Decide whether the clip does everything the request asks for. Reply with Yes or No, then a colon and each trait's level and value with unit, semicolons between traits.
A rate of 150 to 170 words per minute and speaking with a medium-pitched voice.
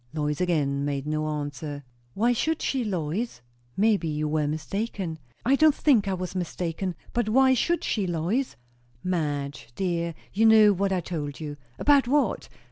Yes: average, 160 wpm; medium, 180 Hz